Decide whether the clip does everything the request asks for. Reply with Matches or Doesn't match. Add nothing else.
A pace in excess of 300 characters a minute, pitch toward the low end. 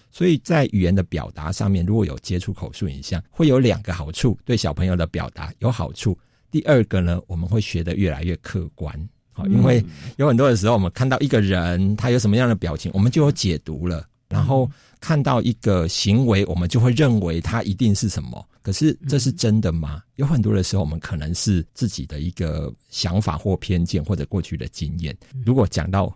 Matches